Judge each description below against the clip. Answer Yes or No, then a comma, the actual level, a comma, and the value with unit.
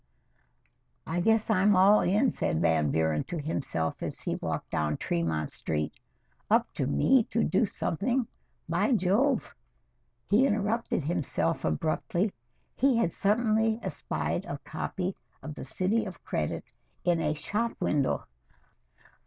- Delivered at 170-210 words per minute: No, slow, 135 wpm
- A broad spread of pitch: Yes, wide, 9.0 semitones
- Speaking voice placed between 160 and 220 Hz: Yes, medium, 185 Hz